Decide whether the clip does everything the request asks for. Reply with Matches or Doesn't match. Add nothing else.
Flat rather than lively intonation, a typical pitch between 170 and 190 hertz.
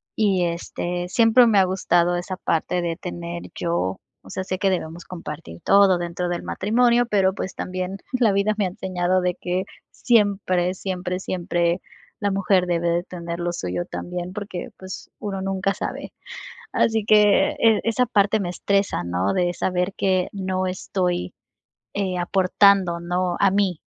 Matches